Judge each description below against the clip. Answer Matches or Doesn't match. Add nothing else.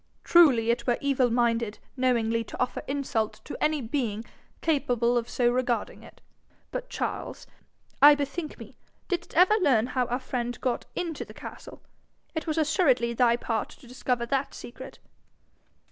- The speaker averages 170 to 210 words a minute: Doesn't match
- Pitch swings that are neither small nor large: Matches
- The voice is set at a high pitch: Matches